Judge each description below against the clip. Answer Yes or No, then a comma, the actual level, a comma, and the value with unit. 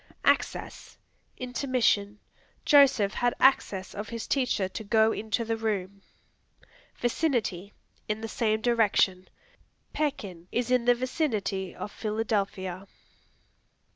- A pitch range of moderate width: Yes, average, 3.5 semitones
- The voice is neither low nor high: No, high, 220 Hz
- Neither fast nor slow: No, slow, 105 wpm